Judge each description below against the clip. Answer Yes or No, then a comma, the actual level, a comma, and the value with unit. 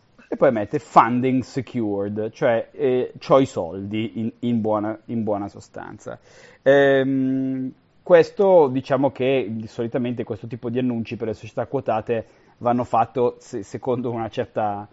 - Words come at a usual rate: Yes, average, 135 wpm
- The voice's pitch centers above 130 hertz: No, low, 120 Hz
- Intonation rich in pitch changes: No, average, 2.9 semitones